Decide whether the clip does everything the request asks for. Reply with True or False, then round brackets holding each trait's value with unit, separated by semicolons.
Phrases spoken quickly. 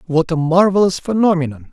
False (140 wpm)